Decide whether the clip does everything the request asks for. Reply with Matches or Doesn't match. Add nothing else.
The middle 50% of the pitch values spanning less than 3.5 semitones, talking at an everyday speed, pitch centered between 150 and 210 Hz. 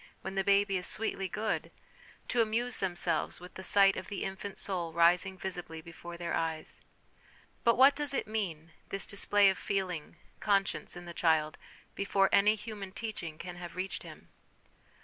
Matches